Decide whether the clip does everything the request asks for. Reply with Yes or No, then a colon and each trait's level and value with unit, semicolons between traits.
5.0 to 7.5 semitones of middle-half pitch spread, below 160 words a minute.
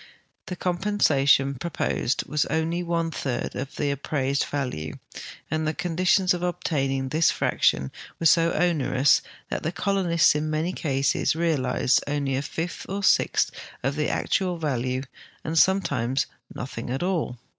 No: average, 4.3 semitones; average, 145 wpm